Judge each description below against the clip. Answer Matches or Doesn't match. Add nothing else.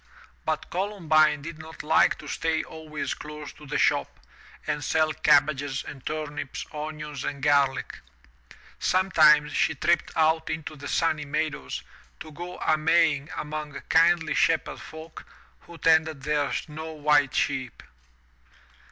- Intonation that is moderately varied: Doesn't match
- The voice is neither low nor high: Matches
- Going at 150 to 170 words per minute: Doesn't match